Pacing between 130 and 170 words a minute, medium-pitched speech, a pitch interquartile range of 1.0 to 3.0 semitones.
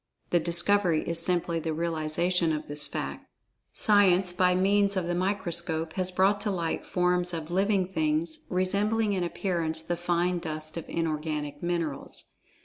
Yes: average, 155 wpm; medium, 175 Hz; narrow, 2.5 semitones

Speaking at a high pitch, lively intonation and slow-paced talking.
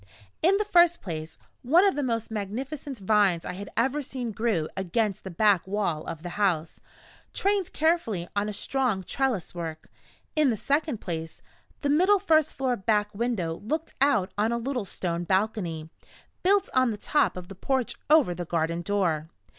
No: high, 215 Hz; wide, 7.4 semitones; average, 175 wpm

